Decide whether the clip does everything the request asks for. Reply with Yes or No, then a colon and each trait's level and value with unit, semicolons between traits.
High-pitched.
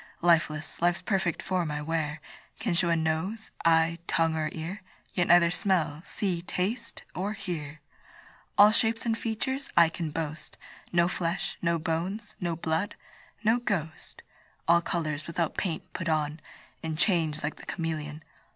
No: medium, 170 Hz